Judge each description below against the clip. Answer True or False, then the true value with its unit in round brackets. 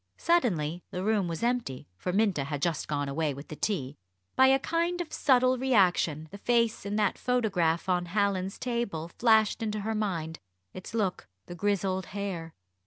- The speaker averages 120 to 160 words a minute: False (175 wpm)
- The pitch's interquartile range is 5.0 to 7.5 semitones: True (5.5 semitones)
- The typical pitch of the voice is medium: False (200 Hz)